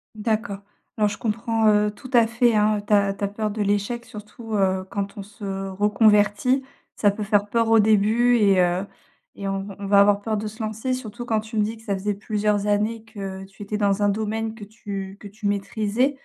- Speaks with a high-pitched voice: Yes, high, 210 Hz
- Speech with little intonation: Yes, narrow, 1.7 semitones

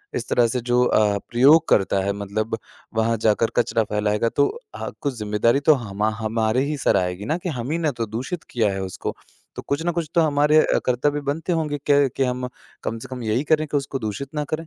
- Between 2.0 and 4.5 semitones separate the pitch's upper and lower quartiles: No, average, 5.0 semitones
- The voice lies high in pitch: No, low, 125 Hz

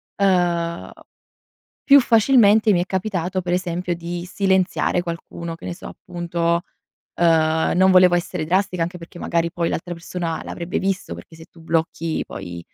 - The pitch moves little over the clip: Yes, narrow, 1.9 semitones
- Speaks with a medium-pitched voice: Yes, medium, 175 Hz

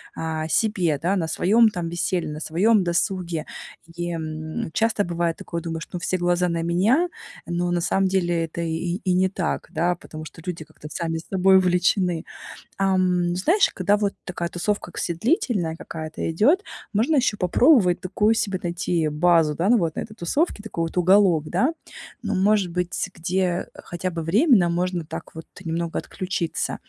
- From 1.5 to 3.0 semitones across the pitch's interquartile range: Yes, average, 2.7 semitones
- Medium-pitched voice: Yes, medium, 175 Hz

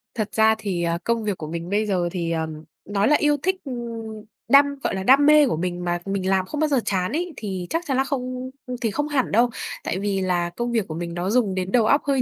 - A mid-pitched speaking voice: No, high, 210 Hz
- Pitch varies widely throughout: Yes, wide, 6.4 semitones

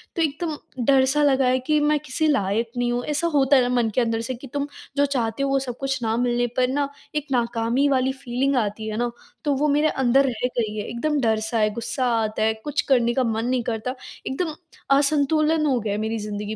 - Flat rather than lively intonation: No, average, 3.6 semitones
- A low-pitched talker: No, very high, 255 Hz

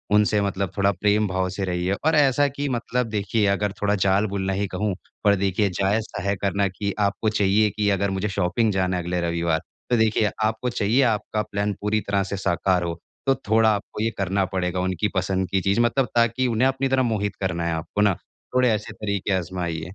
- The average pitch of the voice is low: Yes, low, 100 Hz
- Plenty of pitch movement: No, narrow, 2.5 semitones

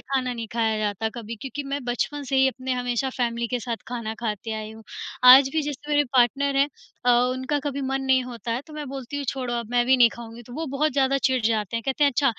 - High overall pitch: Yes, very high, 255 Hz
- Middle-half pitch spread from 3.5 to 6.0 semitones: No, average, 2.7 semitones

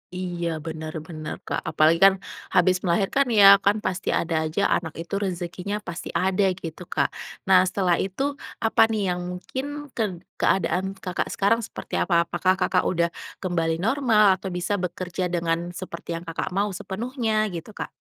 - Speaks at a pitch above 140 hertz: Yes, medium, 185 Hz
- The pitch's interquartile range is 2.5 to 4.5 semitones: Yes, average, 2.8 semitones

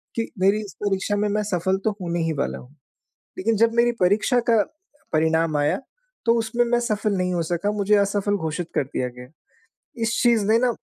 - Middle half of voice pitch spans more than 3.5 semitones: Yes, average, 4.6 semitones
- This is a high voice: Yes, high, 200 Hz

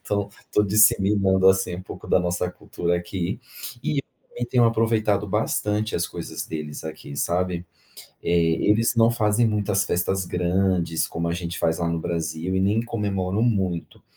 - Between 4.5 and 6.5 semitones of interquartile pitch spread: No, average, 3.5 semitones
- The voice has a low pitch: Yes, very low, 95 Hz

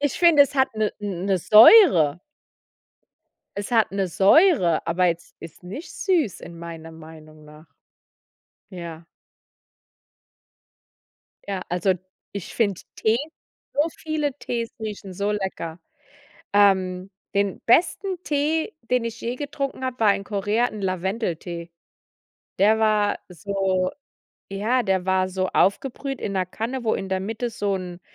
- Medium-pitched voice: No, high, 200 Hz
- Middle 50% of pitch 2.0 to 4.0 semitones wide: No, average, 4.6 semitones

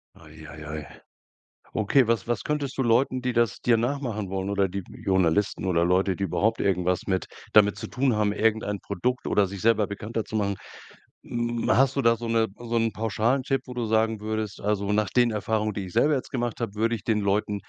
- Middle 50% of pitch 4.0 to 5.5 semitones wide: No, average, 2.9 semitones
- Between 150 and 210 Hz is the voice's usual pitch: No, low, 110 Hz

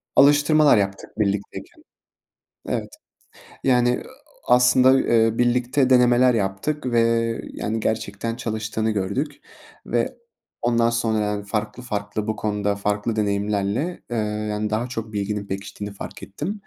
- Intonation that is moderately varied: Yes, average, 3.2 semitones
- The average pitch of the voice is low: Yes, low, 110 Hz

